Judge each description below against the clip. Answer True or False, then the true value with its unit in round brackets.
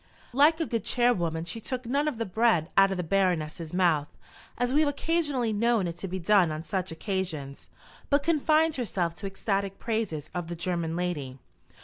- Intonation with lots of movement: True (6.2 semitones)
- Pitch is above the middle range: True (195 Hz)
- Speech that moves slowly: False (190 wpm)